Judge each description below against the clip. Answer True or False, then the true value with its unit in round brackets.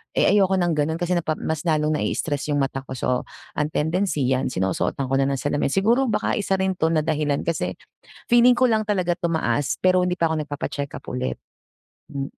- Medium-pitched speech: True (155 Hz)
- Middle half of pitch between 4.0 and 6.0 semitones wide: True (4.5 semitones)